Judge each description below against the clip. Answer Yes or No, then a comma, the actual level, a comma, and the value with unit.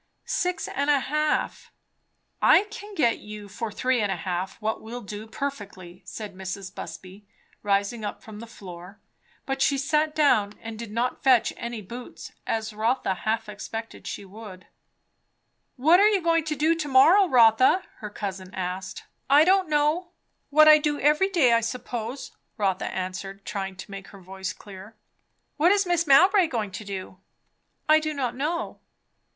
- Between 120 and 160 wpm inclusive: No, average, 170 wpm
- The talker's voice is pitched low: No, high, 230 Hz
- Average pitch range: No, wide, 7.0 semitones